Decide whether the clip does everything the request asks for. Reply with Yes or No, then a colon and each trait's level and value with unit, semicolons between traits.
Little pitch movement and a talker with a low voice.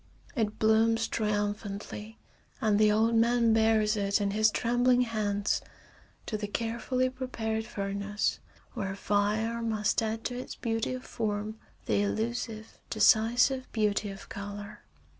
No: narrow, 1.8 semitones; high, 220 Hz